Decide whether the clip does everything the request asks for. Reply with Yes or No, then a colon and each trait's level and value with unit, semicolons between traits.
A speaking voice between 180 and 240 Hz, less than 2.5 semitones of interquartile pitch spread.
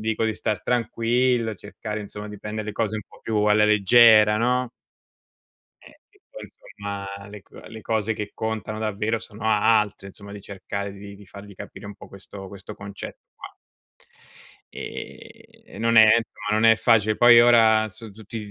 No: low, 110 Hz; narrow, 1.8 semitones